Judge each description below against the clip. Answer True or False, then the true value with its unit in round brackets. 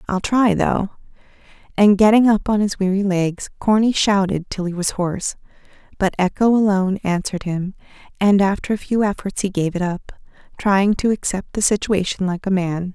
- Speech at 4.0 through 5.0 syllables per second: False (5.2 syllables/s)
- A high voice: True (195 Hz)